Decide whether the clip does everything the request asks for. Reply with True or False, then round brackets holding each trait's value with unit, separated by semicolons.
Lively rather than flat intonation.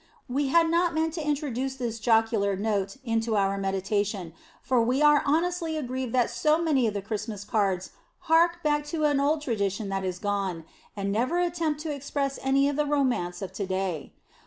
True (6.8 semitones)